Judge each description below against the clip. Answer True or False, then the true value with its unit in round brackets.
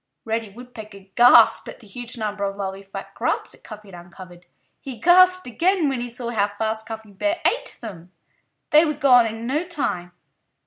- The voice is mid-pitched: False (225 Hz)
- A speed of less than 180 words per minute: False (185 wpm)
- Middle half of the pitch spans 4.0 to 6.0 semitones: True (4.5 semitones)